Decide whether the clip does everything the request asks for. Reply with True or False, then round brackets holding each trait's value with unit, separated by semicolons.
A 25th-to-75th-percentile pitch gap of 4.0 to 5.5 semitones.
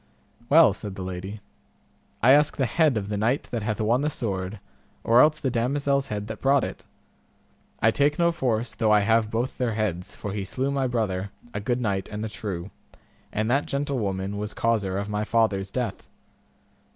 True (4.3 semitones)